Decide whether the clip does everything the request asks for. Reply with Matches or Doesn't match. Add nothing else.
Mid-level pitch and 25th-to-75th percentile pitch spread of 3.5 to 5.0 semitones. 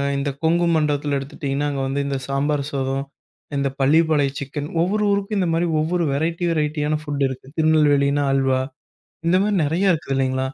Doesn't match